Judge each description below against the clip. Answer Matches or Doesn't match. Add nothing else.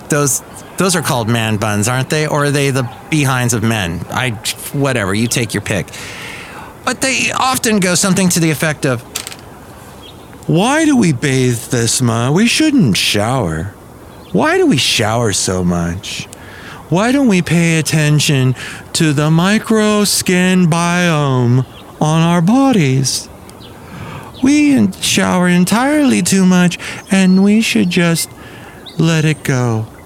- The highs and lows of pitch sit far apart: Matches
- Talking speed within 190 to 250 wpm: Doesn't match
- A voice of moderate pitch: Matches